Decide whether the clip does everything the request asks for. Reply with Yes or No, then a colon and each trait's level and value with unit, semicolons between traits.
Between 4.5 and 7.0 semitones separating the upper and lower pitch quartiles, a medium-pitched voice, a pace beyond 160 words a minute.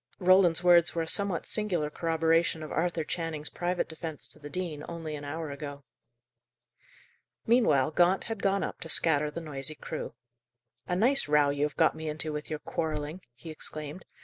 No: average, 2.7 semitones; medium, 160 Hz; average, 175 wpm